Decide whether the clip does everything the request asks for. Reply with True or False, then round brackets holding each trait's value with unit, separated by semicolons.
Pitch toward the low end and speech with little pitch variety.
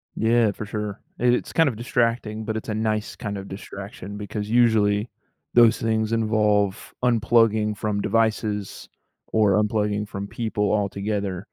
True (105 Hz; 1.7 semitones)